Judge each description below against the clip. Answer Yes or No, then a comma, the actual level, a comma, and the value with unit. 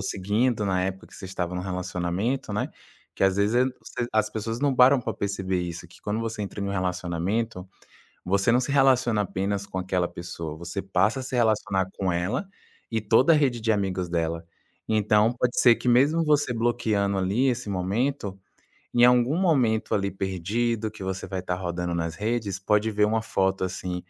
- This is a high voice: No, low, 100 Hz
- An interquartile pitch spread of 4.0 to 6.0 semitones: Yes, average, 4.3 semitones